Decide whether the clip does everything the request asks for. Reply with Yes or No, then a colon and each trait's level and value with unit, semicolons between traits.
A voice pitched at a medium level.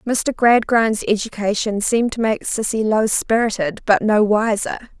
No: high, 215 Hz